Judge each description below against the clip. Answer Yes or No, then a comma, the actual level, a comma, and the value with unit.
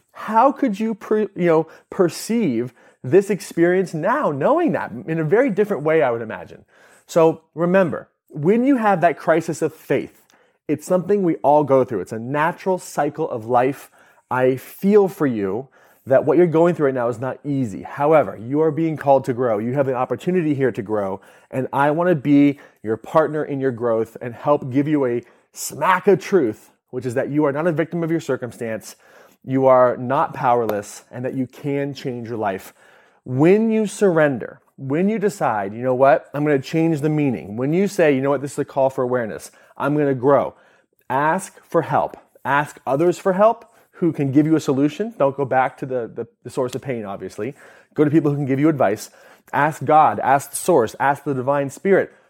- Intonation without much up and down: No, average, 4.3 semitones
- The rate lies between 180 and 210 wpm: Yes, fast, 205 wpm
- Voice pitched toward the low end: No, medium, 145 Hz